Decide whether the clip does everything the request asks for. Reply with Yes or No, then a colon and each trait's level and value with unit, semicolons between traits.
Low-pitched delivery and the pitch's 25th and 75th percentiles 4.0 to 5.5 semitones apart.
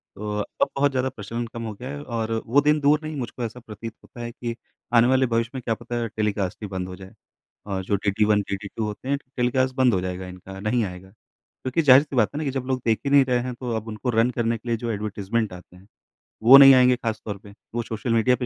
No: low, 115 Hz; average, 3.5 semitones